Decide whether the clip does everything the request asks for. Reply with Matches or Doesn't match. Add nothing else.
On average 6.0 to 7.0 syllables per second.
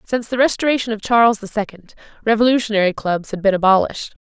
Matches